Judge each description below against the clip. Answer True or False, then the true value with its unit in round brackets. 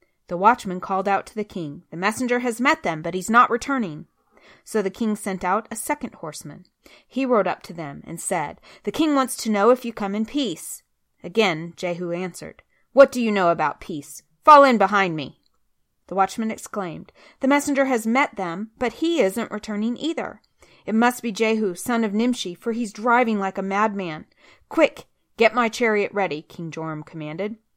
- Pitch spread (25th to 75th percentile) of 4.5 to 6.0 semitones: True (4.8 semitones)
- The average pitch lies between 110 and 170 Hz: False (215 Hz)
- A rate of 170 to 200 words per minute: True (190 wpm)